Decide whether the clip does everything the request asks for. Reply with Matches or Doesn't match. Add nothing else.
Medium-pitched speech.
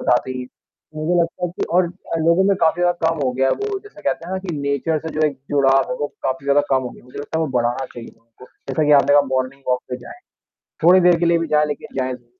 Matches